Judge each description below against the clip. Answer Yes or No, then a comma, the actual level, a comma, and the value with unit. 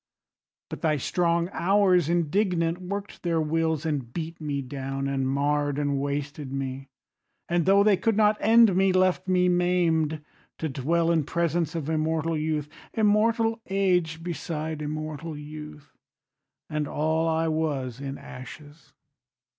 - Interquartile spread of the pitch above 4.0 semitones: No, average, 3.3 semitones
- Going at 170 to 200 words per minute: No, average, 140 wpm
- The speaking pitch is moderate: Yes, medium, 160 Hz